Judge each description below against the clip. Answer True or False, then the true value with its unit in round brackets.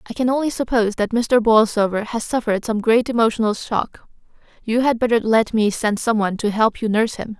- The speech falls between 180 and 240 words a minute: True (205 wpm)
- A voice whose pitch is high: True (225 Hz)